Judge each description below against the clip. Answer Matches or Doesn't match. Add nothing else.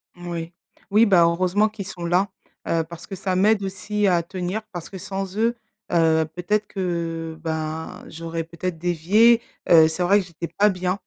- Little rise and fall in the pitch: Doesn't match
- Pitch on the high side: Doesn't match